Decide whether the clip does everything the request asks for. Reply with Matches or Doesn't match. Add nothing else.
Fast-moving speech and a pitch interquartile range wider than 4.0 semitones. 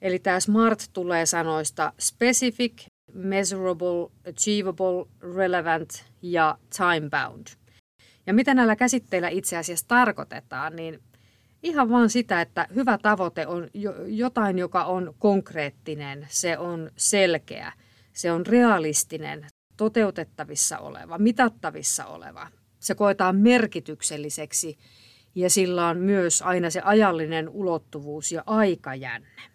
Doesn't match